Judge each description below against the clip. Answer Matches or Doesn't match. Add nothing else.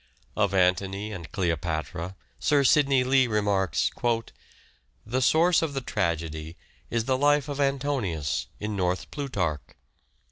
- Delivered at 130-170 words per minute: Matches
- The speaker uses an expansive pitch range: Matches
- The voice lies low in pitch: Matches